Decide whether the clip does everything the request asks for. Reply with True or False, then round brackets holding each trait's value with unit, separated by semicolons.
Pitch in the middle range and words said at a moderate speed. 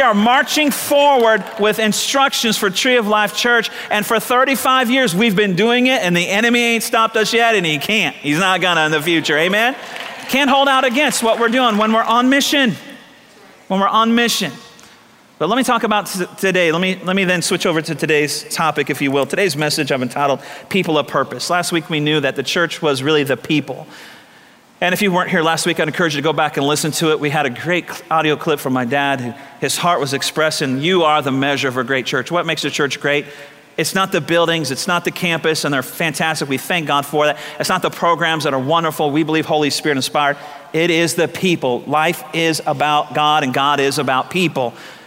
False (165 Hz; 230 wpm)